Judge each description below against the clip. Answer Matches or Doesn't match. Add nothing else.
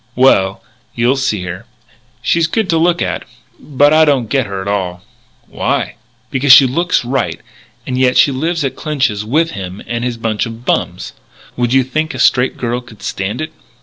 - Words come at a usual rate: Matches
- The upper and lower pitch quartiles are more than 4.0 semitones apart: Matches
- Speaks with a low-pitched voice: Matches